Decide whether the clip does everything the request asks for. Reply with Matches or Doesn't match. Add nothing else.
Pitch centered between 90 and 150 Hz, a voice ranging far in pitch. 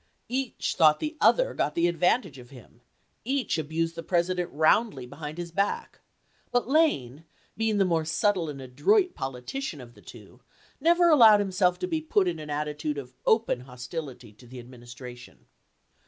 Doesn't match